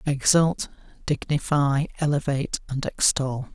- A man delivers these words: Yes, male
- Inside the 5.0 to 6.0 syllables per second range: No, 4.2 syllables/s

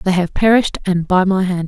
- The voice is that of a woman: Yes, female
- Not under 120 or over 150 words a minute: No, fast, 250 wpm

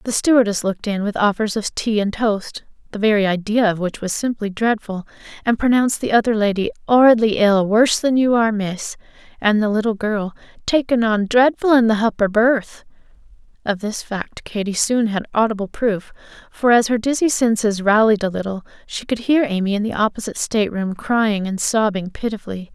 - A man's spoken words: No, female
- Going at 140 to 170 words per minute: No, average, 180 wpm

